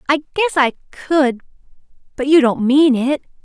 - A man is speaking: No, female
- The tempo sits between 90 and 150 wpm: Yes, average, 140 wpm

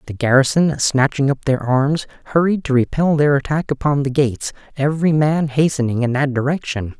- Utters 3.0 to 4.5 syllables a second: No, 5.4 syllables/s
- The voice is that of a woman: No, male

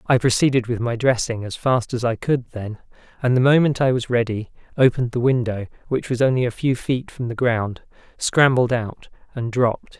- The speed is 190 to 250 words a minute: Yes, average, 200 wpm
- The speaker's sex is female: No, male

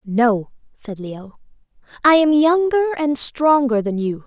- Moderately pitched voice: No, very high, 260 Hz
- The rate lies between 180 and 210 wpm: No, average, 140 wpm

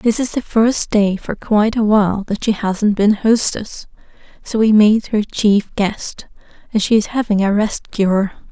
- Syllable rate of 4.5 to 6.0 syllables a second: No, 4.3 syllables/s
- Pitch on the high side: Yes, high, 210 Hz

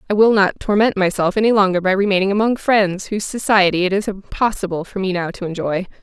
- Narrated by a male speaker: No, female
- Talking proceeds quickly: Yes, fast, 210 wpm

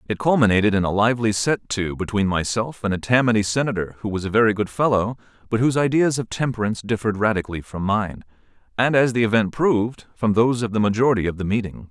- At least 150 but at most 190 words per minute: No, fast, 205 wpm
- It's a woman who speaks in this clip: No, male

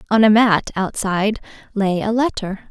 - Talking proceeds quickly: No, average, 155 wpm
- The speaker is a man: No, female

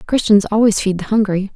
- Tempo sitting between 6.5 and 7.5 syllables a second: No, 5.7 syllables/s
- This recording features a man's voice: No, female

